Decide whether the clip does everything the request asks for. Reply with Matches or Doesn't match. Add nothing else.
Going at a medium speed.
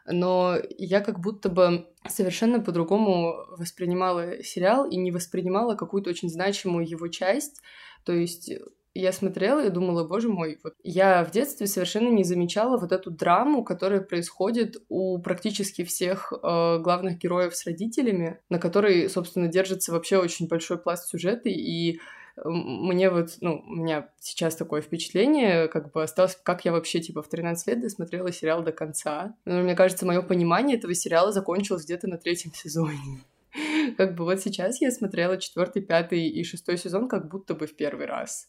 Doesn't match